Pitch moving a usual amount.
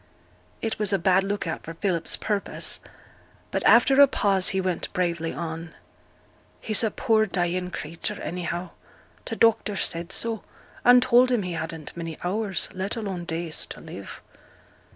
Yes: average, 4.2 semitones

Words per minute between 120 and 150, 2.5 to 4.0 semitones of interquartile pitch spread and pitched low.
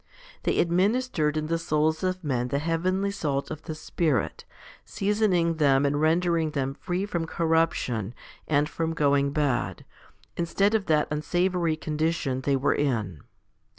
No: average, 145 wpm; average, 3.5 semitones; medium, 155 Hz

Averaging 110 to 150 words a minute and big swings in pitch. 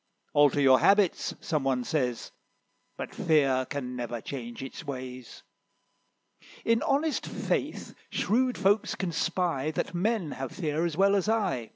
Yes: average, 145 wpm; wide, 7.0 semitones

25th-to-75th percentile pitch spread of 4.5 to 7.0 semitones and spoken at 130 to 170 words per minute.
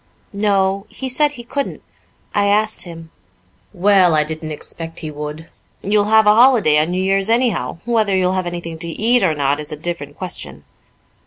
No: average, 4.8 semitones; average, 180 wpm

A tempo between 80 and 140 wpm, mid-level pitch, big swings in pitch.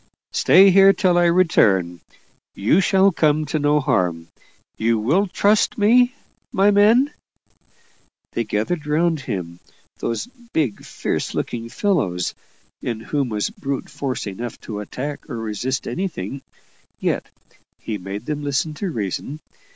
Yes: slow, 135 wpm; medium, 145 Hz; wide, 8.9 semitones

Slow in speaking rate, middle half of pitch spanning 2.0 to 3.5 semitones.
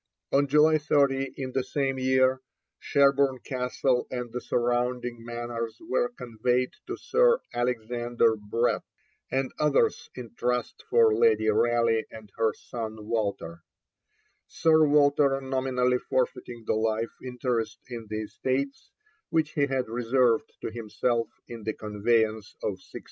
Yes: slow, 130 wpm; average, 2.8 semitones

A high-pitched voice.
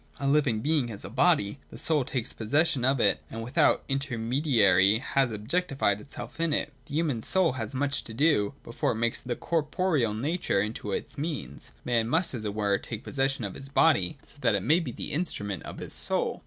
No: low, 130 Hz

